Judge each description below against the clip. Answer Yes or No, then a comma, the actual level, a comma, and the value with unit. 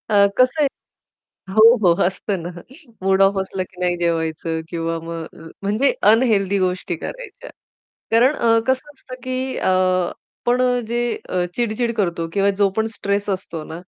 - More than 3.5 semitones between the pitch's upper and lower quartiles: Yes, average, 5.1 semitones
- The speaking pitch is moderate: No, high, 200 Hz